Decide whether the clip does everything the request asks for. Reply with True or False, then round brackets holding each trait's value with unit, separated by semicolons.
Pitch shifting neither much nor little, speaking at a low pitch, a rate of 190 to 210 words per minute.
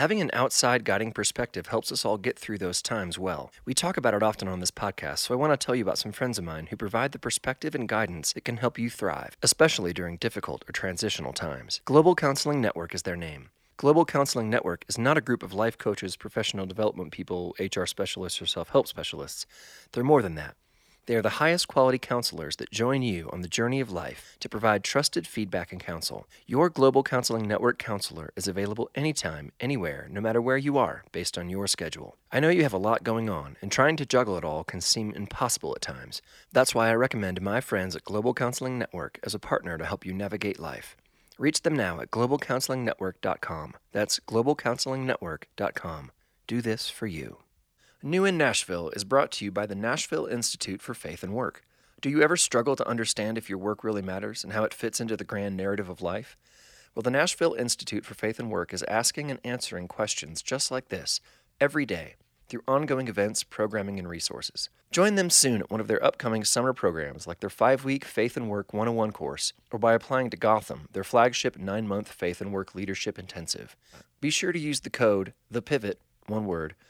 True (4.9 semitones; 110 Hz; 205 wpm)